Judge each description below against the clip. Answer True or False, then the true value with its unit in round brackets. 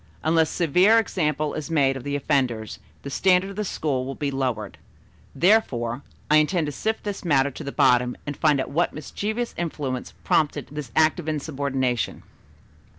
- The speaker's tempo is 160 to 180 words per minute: True (175 wpm)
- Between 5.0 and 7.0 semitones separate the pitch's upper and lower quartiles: False (4.1 semitones)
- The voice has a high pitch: False (150 Hz)